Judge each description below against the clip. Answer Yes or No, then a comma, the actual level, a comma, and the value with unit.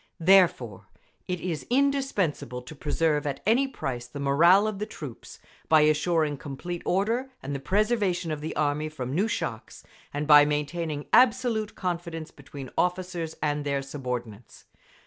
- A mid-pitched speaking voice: Yes, medium, 155 Hz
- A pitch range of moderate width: Yes, average, 4.6 semitones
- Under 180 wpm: Yes, average, 145 wpm